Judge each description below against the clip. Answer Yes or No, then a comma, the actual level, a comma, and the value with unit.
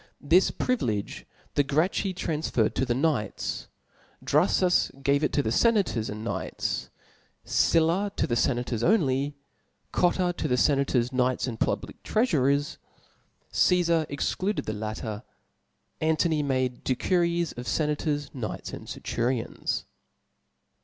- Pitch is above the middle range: No, medium, 145 Hz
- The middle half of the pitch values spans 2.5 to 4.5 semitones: No, wide, 5.5 semitones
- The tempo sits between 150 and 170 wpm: No, slow, 135 wpm